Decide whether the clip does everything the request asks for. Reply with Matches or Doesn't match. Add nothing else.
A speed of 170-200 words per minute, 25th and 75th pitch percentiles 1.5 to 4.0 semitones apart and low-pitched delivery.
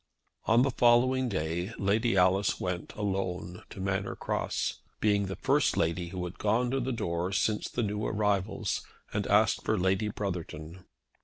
Doesn't match